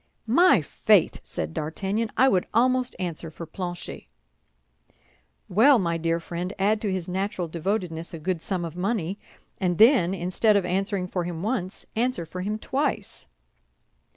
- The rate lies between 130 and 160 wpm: Yes, average, 155 wpm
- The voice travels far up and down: No, average, 3.9 semitones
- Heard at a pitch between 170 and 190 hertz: Yes, medium, 185 Hz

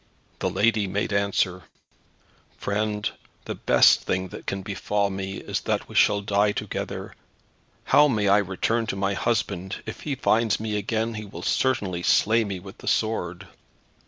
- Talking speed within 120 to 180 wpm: Yes, average, 160 wpm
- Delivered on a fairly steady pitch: Yes, narrow, 2.2 semitones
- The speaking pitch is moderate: No, low, 100 Hz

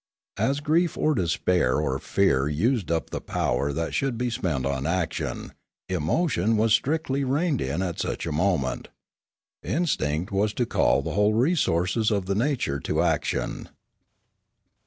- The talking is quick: No, average, 155 wpm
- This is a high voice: No, low, 100 Hz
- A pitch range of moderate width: No, wide, 8.2 semitones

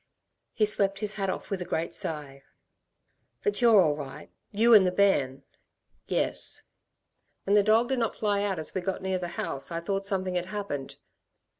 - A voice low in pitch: No, high, 195 Hz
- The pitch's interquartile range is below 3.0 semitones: No, average, 3.5 semitones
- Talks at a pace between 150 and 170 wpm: No, average, 185 wpm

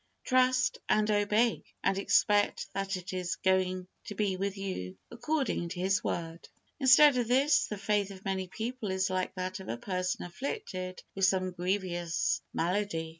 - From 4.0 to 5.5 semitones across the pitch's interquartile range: No, average, 2.7 semitones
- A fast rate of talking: No, average, 165 wpm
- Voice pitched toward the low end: No, high, 195 Hz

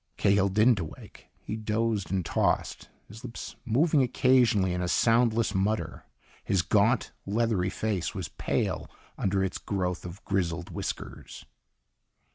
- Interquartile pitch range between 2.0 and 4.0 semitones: Yes, average, 3.5 semitones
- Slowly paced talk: Yes, slow, 130 wpm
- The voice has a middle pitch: No, low, 100 Hz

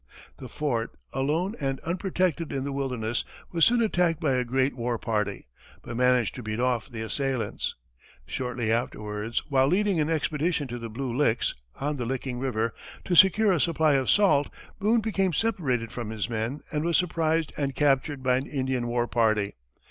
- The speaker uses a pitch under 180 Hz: Yes, low, 135 Hz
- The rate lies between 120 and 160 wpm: No, average, 180 wpm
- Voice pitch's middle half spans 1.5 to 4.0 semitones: No, average, 5.2 semitones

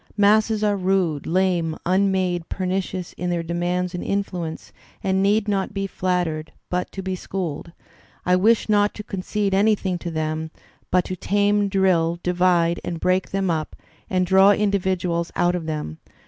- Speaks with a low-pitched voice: No, medium, 185 Hz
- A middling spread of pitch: No, narrow, 2.3 semitones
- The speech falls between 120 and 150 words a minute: No, average, 160 wpm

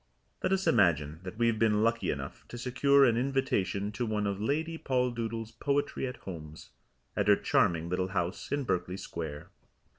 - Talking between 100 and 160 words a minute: No, average, 175 wpm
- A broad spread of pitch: Yes, wide, 5.7 semitones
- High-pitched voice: No, low, 110 Hz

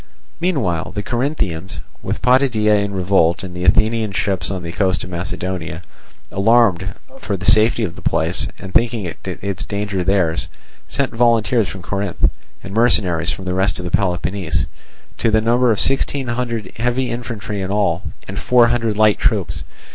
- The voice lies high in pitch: No, low, 100 Hz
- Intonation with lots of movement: No, average, 4.2 semitones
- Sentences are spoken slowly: No, average, 160 wpm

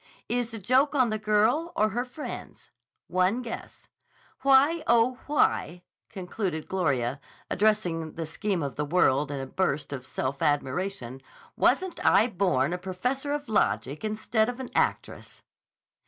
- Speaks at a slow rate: No, average, 145 wpm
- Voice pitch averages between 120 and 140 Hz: No, high, 195 Hz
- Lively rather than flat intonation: Yes, wide, 7.9 semitones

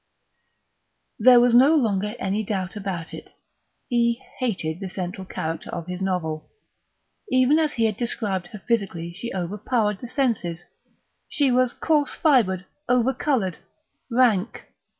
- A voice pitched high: Yes, high, 210 Hz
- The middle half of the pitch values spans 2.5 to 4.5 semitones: No, average, 5.1 semitones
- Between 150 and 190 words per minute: No, slow, 135 wpm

